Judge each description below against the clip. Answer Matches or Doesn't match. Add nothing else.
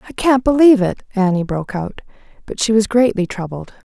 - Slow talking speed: Doesn't match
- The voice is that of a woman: Matches